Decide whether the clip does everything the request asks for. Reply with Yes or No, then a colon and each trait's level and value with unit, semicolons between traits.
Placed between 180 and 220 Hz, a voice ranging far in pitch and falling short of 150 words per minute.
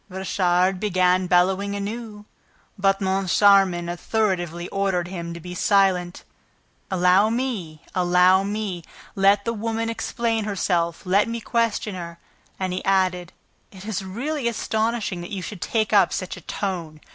No: high, 190 Hz; average, 2.8 semitones; average, 140 wpm